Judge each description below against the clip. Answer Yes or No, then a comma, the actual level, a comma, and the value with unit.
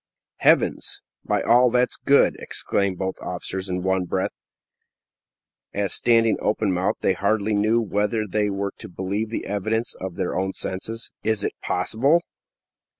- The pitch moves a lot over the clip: No, average, 2.9 semitones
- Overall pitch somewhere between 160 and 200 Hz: No, low, 105 Hz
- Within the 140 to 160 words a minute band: Yes, average, 150 wpm